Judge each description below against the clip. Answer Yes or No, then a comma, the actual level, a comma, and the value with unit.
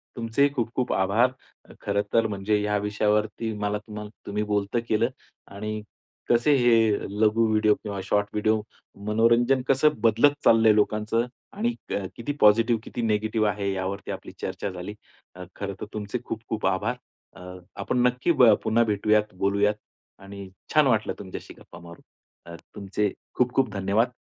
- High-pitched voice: No, low, 105 Hz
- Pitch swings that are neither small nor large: No, narrow, 2.2 semitones